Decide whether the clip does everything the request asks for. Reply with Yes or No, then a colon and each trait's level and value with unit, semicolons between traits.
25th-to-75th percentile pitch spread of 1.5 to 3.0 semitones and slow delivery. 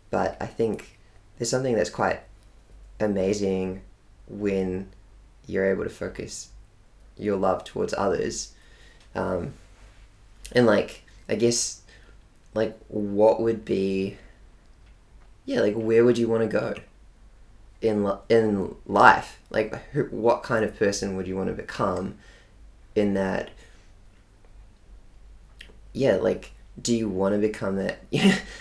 Yes: narrow, 2.4 semitones; slow, 125 wpm